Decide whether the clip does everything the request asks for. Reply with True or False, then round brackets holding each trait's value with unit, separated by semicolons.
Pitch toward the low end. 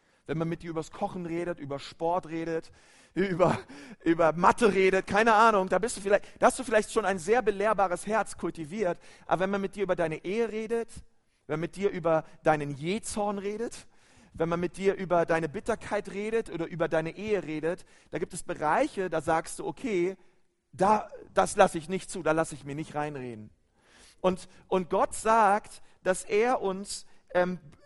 False (180 Hz)